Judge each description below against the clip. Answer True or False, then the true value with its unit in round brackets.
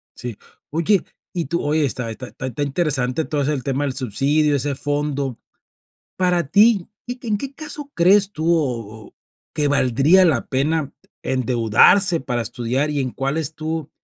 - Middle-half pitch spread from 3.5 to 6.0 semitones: True (4.5 semitones)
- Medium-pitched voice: True (145 Hz)